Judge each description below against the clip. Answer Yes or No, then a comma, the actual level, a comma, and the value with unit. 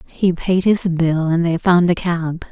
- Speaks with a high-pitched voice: No, medium, 175 Hz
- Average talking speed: No, fast, 215 wpm